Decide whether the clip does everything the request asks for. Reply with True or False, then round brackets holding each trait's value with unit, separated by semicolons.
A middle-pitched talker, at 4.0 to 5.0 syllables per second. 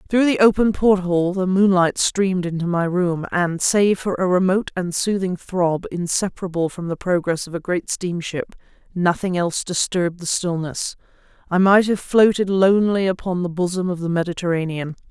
False (180 Hz; 5.2 syllables/s)